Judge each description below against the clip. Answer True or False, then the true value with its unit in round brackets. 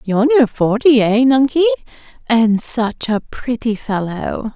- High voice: True (235 Hz)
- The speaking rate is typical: False (130 wpm)